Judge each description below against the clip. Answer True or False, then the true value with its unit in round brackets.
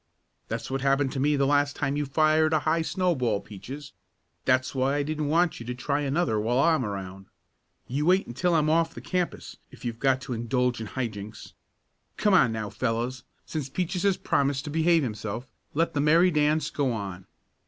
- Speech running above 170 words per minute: True (195 wpm)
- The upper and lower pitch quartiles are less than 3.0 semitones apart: False (4.6 semitones)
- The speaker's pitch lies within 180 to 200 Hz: False (140 Hz)